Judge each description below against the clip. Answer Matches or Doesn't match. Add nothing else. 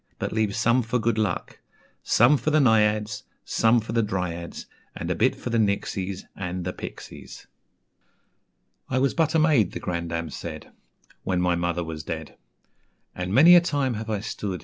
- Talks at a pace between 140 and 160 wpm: Doesn't match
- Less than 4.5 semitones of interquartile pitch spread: Doesn't match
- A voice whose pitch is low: Matches